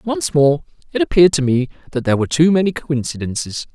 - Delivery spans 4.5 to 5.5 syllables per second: No, 6.4 syllables/s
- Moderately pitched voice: Yes, medium, 150 Hz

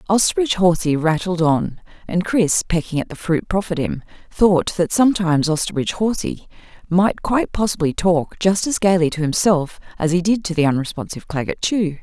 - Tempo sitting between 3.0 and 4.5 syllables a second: No, 5.6 syllables/s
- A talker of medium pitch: Yes, medium, 175 Hz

